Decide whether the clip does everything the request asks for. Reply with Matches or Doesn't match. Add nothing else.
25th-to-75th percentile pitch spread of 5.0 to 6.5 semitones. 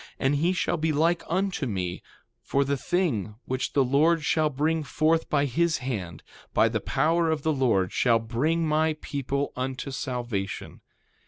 Doesn't match